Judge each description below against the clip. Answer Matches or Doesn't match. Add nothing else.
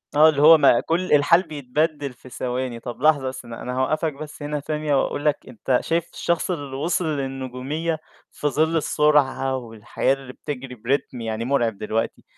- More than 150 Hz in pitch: Doesn't match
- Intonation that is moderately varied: Matches